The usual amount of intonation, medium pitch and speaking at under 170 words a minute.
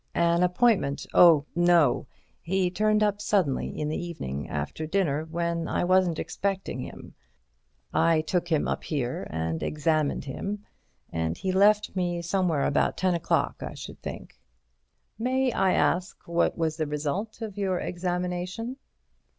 Yes: average, 3.6 semitones; medium, 175 Hz; average, 145 wpm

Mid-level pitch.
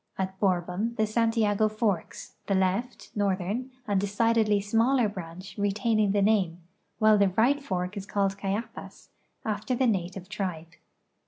No: high, 205 Hz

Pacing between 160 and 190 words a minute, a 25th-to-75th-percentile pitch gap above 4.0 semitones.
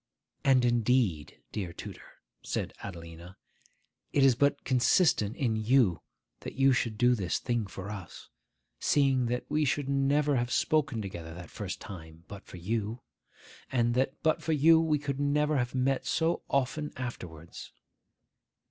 No: average, 150 wpm; wide, 5.6 semitones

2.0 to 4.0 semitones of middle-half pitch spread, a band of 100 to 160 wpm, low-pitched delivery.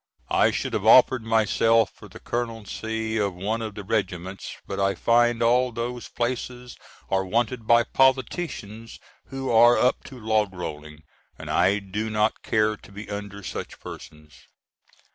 Yes: average, 3.0 semitones; average, 155 wpm; low, 110 Hz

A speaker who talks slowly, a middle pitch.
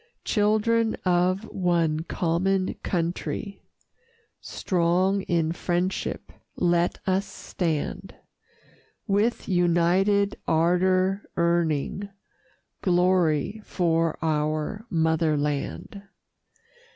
Yes: slow, 70 wpm; medium, 175 Hz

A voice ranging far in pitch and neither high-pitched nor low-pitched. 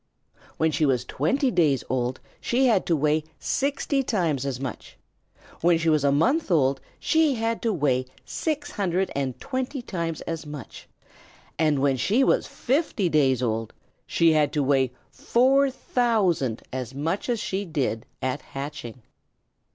Yes: wide, 9.0 semitones; medium, 160 Hz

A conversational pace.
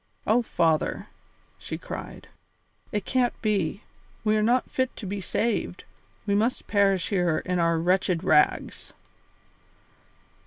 No: slow, 125 wpm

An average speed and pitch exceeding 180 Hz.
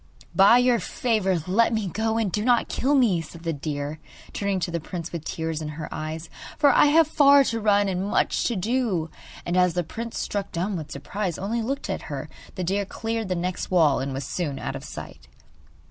No: fast, 215 wpm; high, 190 Hz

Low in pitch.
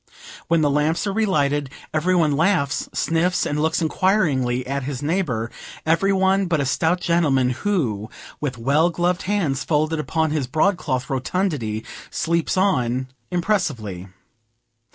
No: medium, 155 Hz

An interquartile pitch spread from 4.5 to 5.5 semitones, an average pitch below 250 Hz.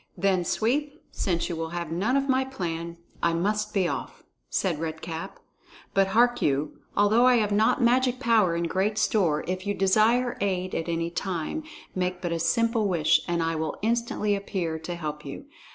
Yes: average, 4.9 semitones; high, 190 Hz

